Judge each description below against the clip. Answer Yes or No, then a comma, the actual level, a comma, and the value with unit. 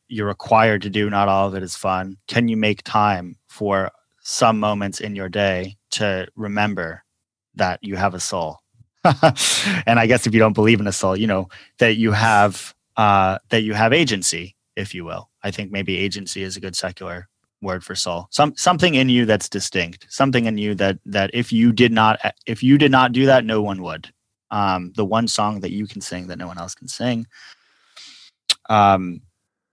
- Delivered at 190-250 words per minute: Yes, average, 200 wpm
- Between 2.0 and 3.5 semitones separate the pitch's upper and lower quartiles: Yes, average, 2.9 semitones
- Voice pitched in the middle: No, low, 105 Hz